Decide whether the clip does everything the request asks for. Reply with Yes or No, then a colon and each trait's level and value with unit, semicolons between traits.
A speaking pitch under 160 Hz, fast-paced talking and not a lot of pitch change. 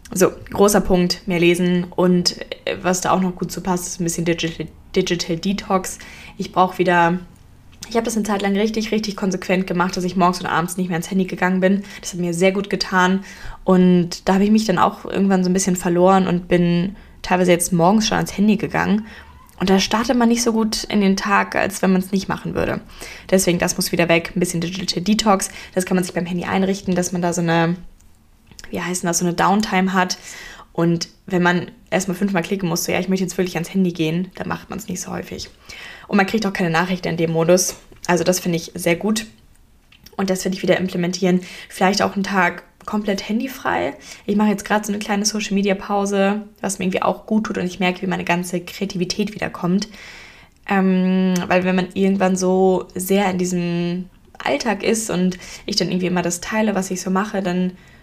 No: medium, 185 Hz; fast, 215 wpm; narrow, 1.9 semitones